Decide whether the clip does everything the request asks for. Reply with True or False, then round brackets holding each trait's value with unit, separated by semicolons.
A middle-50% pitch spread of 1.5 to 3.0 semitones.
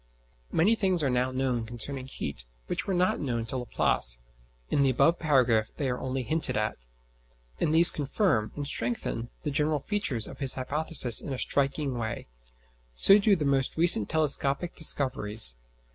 False (4.8 semitones)